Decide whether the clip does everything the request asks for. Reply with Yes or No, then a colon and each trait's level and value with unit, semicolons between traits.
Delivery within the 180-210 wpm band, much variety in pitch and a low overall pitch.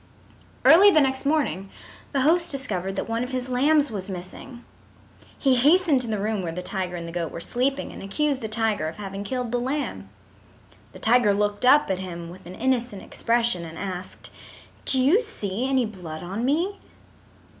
No: average, 185 wpm; wide, 6.2 semitones; high, 230 Hz